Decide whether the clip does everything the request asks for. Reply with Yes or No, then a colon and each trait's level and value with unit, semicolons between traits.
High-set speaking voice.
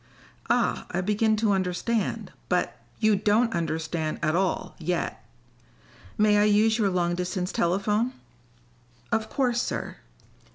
Yes: high, 200 Hz